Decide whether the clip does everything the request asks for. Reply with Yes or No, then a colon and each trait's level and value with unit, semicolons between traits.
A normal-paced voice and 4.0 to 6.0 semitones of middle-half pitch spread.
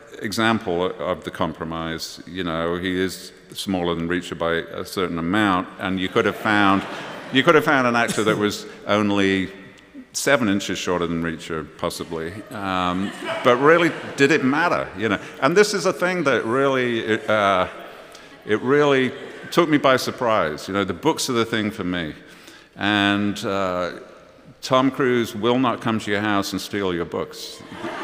Yes: average, 170 wpm; average, 4.3 semitones